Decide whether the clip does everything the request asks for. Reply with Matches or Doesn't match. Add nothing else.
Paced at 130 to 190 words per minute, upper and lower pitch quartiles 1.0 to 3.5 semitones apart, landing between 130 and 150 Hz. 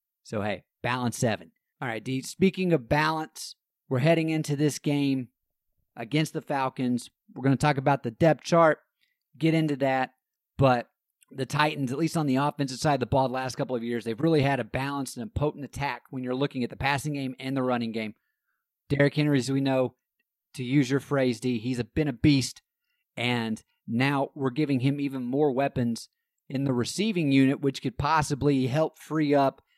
Doesn't match